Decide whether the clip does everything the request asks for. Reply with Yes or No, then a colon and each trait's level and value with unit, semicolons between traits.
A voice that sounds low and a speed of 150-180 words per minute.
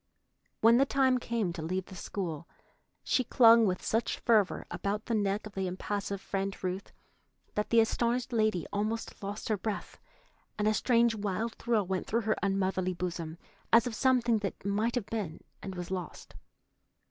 No: high, 210 Hz; average, 170 wpm